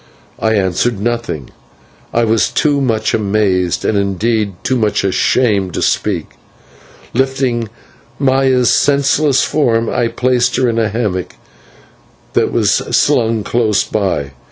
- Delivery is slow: Yes, slow, 125 wpm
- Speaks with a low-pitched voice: Yes, low, 115 Hz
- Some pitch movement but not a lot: Yes, average, 3.7 semitones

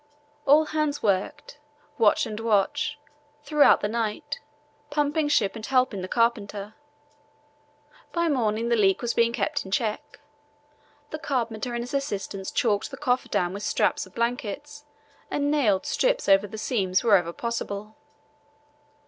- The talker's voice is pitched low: No, high, 235 Hz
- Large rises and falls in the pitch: Yes, wide, 5.7 semitones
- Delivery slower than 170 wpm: Yes, average, 140 wpm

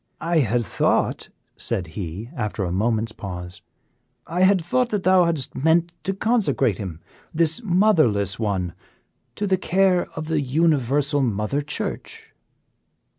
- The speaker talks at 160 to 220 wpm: No, slow, 135 wpm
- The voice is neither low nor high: Yes, medium, 145 Hz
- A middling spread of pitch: No, wide, 8.6 semitones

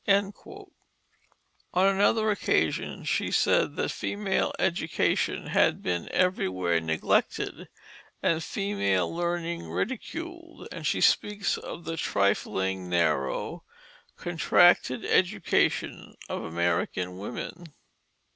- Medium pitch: Yes, medium, 170 Hz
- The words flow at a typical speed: No, slow, 90 wpm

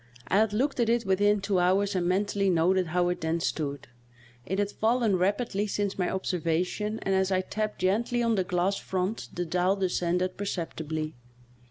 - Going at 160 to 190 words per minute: Yes, average, 185 wpm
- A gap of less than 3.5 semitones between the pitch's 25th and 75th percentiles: Yes, narrow, 2.5 semitones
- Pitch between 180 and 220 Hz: Yes, high, 190 Hz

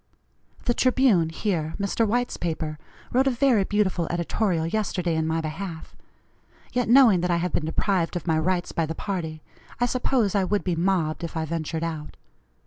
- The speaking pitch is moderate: Yes, medium, 175 Hz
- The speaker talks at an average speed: Yes, average, 180 wpm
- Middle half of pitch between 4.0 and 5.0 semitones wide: Yes, average, 4.6 semitones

